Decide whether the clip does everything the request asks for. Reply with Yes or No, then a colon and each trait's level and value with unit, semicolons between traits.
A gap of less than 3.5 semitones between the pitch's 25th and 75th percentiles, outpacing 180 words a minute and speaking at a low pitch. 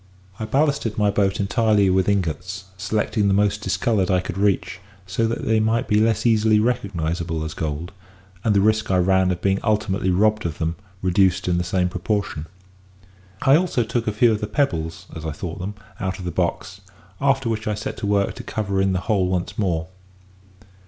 Yes: average, 3.1 semitones; average, 200 wpm; low, 100 Hz